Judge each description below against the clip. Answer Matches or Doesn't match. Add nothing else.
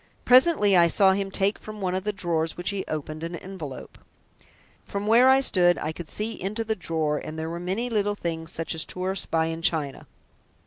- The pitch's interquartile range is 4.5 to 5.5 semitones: Doesn't match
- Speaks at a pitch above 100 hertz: Matches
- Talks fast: Matches